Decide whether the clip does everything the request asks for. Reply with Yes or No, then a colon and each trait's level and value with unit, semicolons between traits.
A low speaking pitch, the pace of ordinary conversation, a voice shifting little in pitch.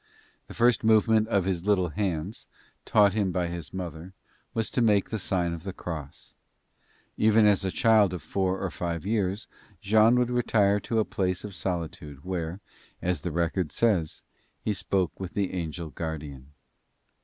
No: very low, 95 Hz; average, 165 wpm; average, 3.6 semitones